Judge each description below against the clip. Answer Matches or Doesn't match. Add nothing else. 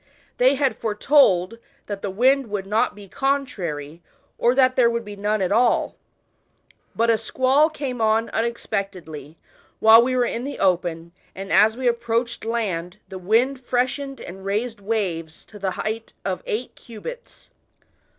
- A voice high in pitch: Matches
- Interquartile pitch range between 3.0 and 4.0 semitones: Doesn't match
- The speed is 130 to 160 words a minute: Matches